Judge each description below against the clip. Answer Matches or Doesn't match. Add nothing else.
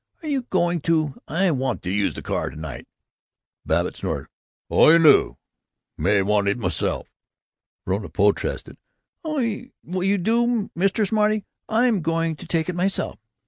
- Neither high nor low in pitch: Matches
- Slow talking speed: Doesn't match